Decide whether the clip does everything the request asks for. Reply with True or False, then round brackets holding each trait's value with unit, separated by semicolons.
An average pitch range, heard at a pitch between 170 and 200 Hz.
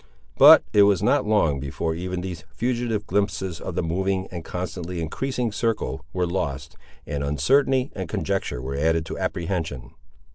False (4.4 semitones; 90 Hz)